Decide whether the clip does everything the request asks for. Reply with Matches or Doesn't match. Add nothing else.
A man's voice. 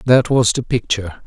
Matches